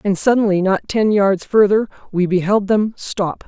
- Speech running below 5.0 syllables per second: Yes, 4.5 syllables/s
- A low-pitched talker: No, high, 200 Hz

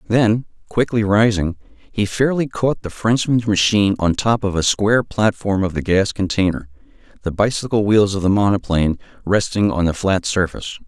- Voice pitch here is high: No, low, 100 Hz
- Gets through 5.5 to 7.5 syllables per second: No, 5.2 syllables/s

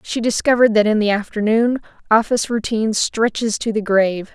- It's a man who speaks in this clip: No, female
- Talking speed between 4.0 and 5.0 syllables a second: No, 5.8 syllables/s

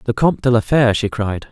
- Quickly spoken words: Yes, fast, 280 wpm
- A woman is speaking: No, male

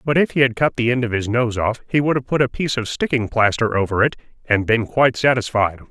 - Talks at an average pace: No, fast, 265 wpm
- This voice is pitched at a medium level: No, low, 120 Hz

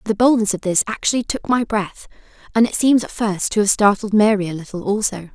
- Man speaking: No, female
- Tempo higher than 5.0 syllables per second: Yes, 5.8 syllables/s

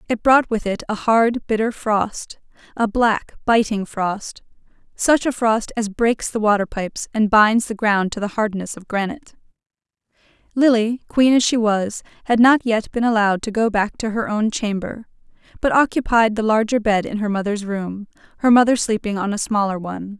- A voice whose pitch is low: No, high, 220 Hz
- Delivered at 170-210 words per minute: Yes, average, 180 wpm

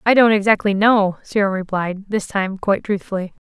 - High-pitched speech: Yes, high, 200 Hz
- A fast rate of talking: No, average, 175 wpm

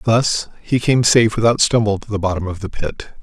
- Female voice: No, male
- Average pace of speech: No, fast, 225 wpm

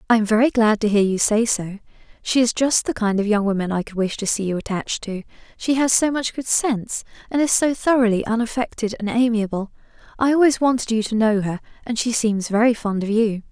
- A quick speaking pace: Yes, fast, 230 wpm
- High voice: Yes, high, 225 Hz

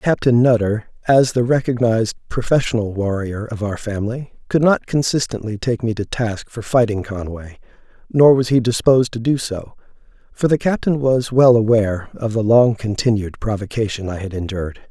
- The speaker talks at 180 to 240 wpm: No, average, 165 wpm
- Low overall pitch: Yes, low, 115 Hz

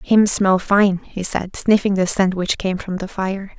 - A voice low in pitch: No, high, 190 Hz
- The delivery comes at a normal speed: No, fast, 215 wpm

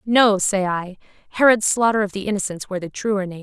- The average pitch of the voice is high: Yes, high, 200 Hz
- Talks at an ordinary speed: No, fast, 210 wpm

